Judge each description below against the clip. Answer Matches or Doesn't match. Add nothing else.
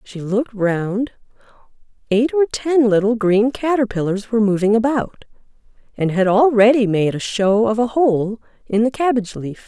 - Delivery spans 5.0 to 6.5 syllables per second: Doesn't match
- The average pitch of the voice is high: Matches